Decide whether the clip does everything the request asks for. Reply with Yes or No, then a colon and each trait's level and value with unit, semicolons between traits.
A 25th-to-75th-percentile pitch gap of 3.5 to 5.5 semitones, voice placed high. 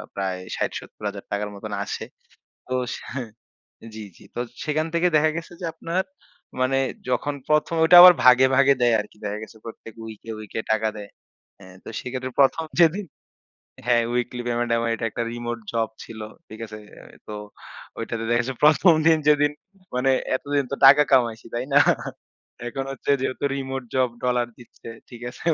No: average, 3.9 semitones; low, 125 Hz